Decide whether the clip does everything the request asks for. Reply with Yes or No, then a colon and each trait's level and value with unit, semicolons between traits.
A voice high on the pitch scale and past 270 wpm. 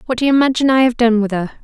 Yes: high, 240 Hz; fast, 330 wpm